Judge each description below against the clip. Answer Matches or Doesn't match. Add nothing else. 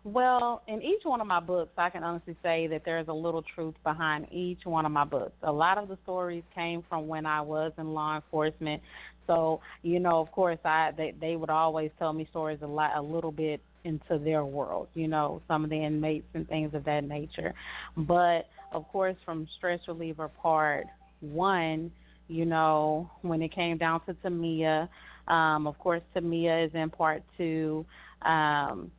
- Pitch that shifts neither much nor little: Doesn't match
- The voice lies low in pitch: Doesn't match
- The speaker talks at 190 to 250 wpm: Matches